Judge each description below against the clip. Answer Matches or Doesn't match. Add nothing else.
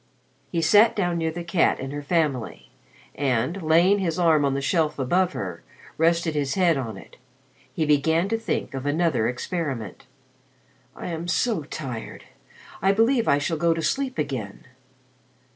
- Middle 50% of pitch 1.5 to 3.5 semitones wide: Doesn't match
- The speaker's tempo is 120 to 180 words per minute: Matches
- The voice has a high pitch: Doesn't match